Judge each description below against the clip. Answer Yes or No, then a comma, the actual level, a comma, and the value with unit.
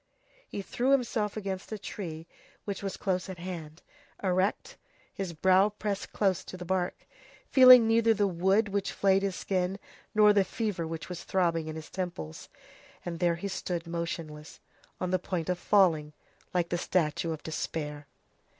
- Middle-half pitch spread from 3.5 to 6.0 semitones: No, average, 3.1 semitones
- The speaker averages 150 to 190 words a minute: Yes, average, 165 wpm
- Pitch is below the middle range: No, medium, 185 Hz